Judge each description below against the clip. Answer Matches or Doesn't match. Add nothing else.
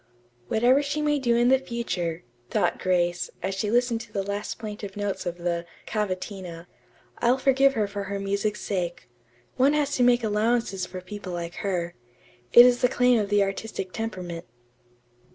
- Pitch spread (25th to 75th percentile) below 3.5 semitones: Doesn't match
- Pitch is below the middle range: Doesn't match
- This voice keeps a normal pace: Matches